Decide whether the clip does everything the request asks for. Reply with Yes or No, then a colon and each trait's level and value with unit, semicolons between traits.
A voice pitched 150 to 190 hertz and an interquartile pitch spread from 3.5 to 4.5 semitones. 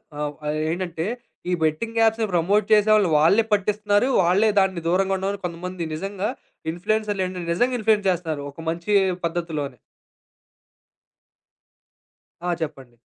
Yes: medium, 185 Hz; average, 4.0 semitones